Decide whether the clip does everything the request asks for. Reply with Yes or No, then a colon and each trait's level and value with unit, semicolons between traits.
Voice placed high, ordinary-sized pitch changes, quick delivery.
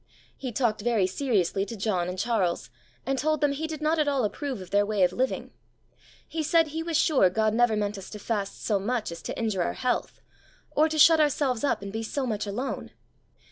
No: high, 230 Hz; wide, 6.1 semitones; fast, 220 wpm